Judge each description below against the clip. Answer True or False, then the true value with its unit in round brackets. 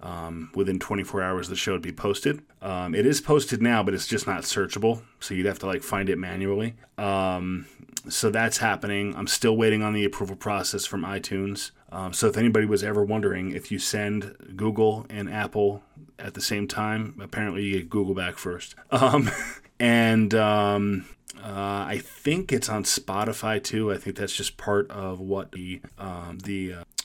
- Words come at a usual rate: True (190 wpm)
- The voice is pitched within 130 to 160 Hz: False (100 Hz)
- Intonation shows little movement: True (2.2 semitones)